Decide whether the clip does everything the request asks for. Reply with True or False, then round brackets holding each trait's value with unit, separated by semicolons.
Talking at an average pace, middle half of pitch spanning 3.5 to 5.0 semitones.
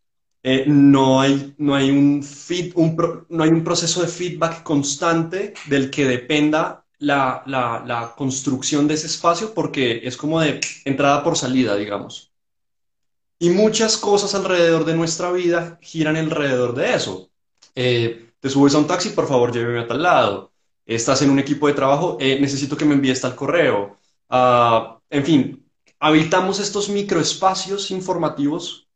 True (160 wpm; 4.2 semitones)